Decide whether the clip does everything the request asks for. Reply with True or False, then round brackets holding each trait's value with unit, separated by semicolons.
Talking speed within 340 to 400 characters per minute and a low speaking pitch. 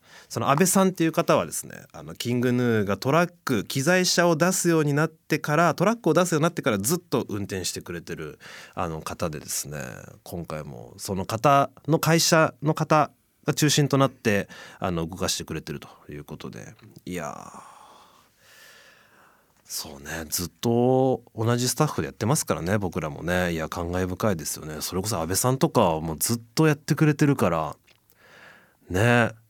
True (350 characters per minute; 125 Hz)